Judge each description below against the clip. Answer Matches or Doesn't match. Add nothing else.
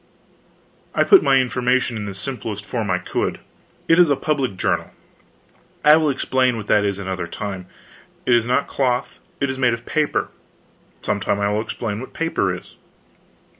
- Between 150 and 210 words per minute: Matches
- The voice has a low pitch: Matches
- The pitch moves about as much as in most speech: Matches